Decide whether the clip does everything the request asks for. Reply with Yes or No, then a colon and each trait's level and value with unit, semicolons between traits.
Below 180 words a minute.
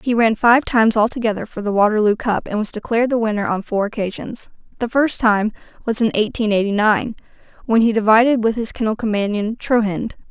No: average, 190 wpm